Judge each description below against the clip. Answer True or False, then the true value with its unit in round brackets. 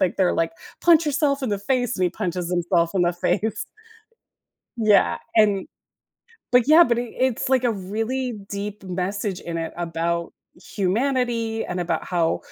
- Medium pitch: False (205 Hz)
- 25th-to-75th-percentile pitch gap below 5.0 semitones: False (5.6 semitones)